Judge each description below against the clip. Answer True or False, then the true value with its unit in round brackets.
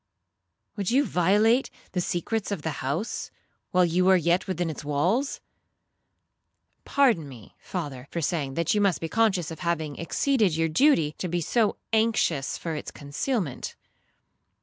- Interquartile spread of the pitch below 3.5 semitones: False (5.2 semitones)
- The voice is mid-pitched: True (175 Hz)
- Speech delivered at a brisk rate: False (150 wpm)